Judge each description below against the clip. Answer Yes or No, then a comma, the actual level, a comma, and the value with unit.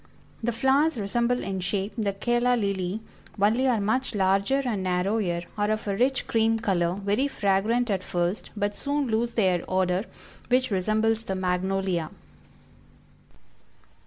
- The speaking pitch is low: No, high, 205 Hz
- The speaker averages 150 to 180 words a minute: No, average, 140 wpm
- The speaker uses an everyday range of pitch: Yes, average, 3.8 semitones